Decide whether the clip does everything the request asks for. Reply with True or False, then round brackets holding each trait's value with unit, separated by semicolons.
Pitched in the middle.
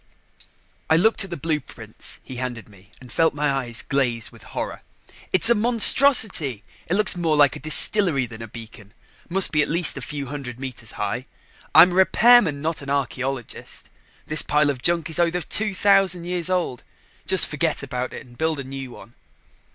True (150 Hz)